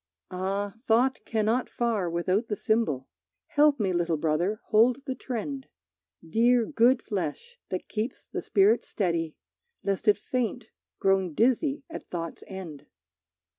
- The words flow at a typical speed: No, slow, 130 wpm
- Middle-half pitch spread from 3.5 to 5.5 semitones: Yes, average, 5.0 semitones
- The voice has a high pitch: Yes, high, 215 Hz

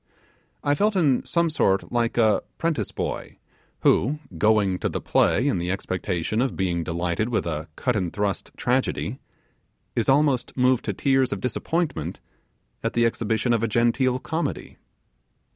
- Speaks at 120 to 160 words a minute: Yes, average, 155 wpm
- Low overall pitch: Yes, low, 115 Hz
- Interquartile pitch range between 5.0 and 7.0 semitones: Yes, wide, 5.6 semitones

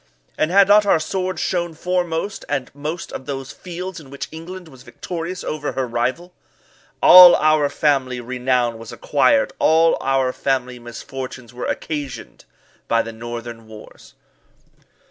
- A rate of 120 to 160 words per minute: Yes, average, 145 wpm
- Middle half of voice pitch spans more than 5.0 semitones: Yes, wide, 5.4 semitones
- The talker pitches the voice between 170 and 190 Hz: No, medium, 140 Hz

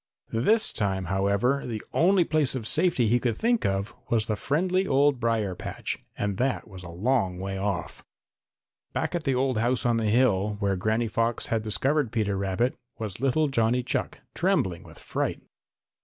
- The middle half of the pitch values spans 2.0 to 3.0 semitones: No, average, 5.0 semitones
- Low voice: Yes, low, 115 Hz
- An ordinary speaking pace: Yes, average, 175 wpm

